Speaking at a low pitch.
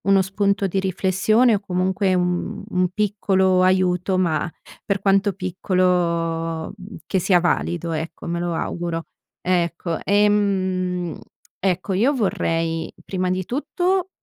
No: medium, 185 Hz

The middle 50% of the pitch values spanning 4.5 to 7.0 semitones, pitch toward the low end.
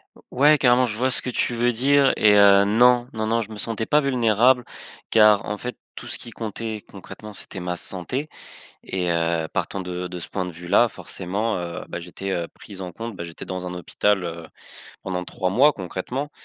Yes: average, 5.0 semitones; low, 105 Hz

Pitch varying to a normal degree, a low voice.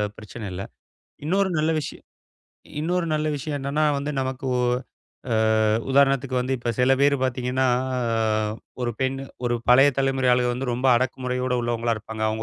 No: narrow, 2.3 semitones; low, 130 Hz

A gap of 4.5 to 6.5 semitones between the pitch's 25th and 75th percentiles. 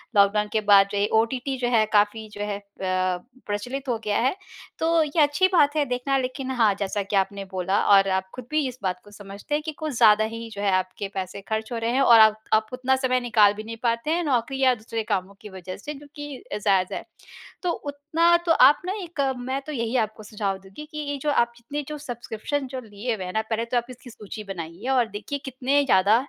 Yes: average, 4.8 semitones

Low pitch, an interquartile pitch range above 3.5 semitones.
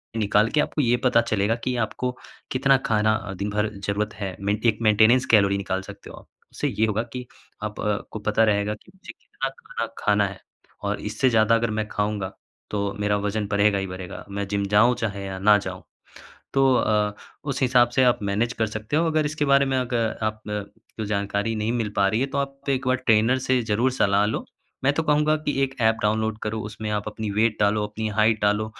No: low, 110 Hz; average, 3.2 semitones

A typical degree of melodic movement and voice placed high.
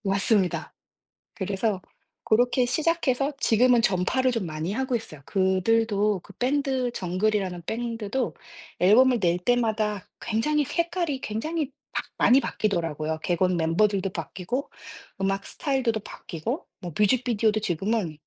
Yes: average, 5.0 semitones; high, 215 Hz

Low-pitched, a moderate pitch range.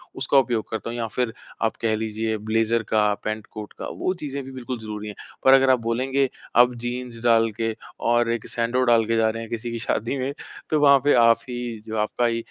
No: low, 115 Hz; narrow, 2.2 semitones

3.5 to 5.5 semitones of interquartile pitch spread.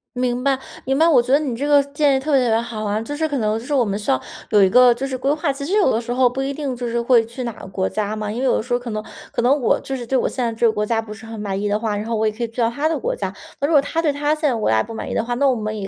Yes: average, 3.8 semitones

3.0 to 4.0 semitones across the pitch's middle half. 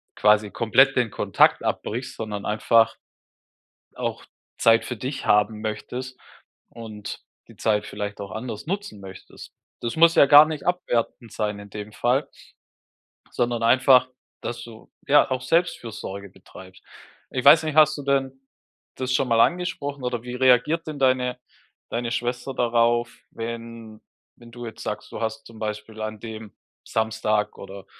Yes: average, 3.3 semitones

